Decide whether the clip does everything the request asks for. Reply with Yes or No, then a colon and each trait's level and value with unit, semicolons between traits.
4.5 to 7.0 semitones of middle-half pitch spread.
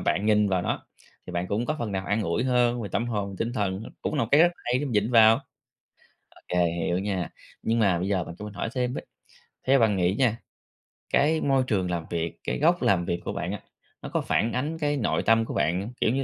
Yes: average, 5.0 semitones